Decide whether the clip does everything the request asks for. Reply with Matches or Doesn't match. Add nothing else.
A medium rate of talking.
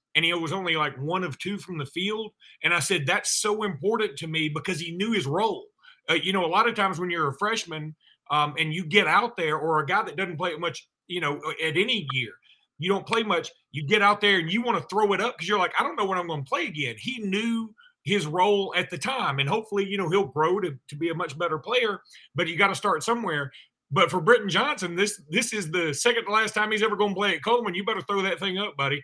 Doesn't match